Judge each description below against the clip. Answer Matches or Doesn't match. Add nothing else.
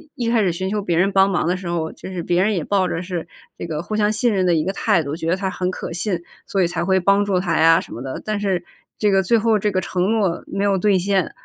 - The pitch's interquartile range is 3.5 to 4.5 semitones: Doesn't match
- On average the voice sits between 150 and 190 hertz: Matches